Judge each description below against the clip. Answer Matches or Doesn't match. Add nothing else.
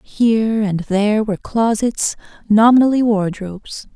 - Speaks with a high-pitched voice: Matches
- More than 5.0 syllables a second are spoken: Doesn't match